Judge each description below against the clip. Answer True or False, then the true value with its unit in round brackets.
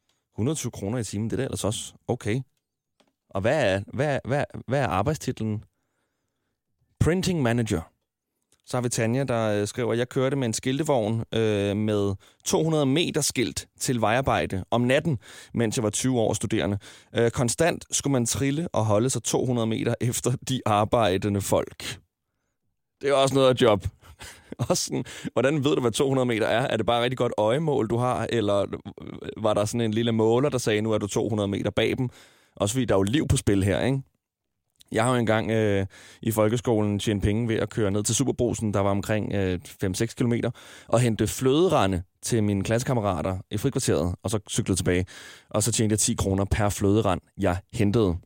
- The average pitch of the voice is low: True (110 Hz)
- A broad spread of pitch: False (3.4 semitones)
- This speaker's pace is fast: False (190 wpm)